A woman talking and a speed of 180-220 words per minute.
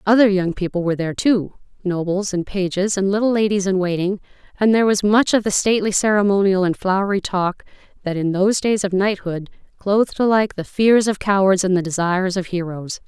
Yes: female; average, 190 wpm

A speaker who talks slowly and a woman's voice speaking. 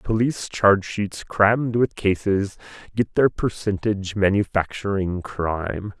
No: slow, 100 wpm; male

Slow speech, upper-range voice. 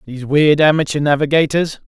No: slow, 125 wpm; medium, 150 Hz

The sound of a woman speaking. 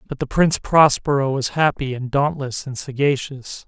No: male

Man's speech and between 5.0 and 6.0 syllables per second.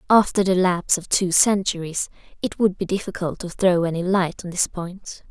No: female; 5.1 syllables/s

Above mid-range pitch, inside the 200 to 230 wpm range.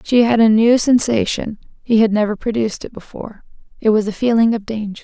Yes: high, 220 Hz; fast, 205 wpm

